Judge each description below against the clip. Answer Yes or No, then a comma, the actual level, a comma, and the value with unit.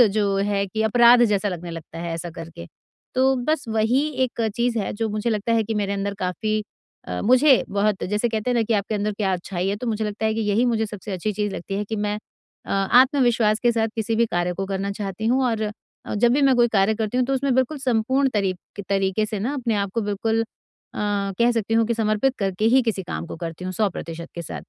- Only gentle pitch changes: No, average, 3.1 semitones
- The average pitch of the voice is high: Yes, high, 215 Hz